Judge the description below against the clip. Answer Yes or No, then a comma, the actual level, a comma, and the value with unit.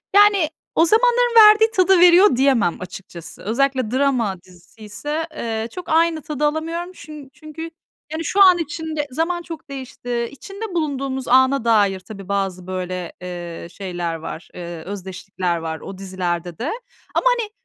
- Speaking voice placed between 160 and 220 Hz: No, very high, 260 Hz